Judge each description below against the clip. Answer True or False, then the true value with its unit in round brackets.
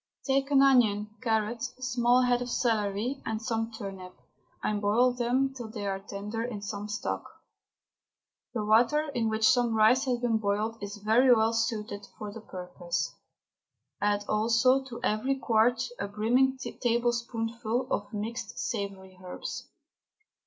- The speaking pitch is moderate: False (225 Hz)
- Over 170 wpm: False (145 wpm)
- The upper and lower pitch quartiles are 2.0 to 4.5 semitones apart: True (2.9 semitones)